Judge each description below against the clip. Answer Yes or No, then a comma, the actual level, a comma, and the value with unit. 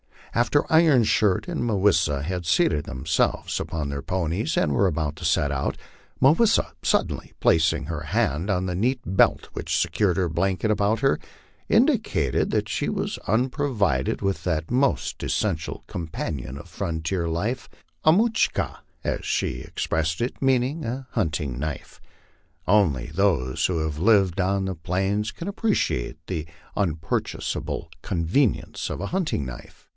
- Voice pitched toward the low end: Yes, very low, 90 Hz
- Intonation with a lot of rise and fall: Yes, wide, 6.0 semitones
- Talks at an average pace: Yes, average, 155 wpm